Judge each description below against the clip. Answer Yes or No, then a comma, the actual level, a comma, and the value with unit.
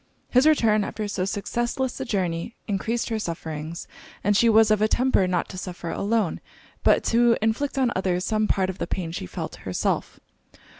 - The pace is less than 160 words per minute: No, average, 185 wpm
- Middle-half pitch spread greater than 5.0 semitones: No, average, 4.1 semitones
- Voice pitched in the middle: No, high, 210 Hz